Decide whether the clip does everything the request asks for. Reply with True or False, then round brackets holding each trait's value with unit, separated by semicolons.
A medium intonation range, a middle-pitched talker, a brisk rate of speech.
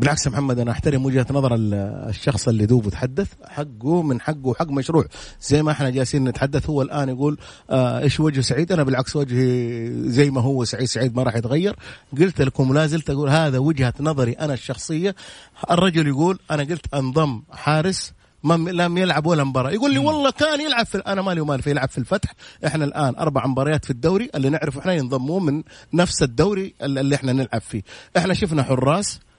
True (3.7 semitones; 145 Hz; 185 wpm)